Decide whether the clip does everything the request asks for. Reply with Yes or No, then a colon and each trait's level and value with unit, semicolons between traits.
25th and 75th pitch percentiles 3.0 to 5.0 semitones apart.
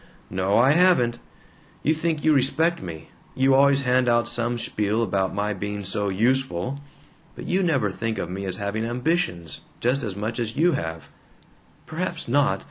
No: wide, 5.6 semitones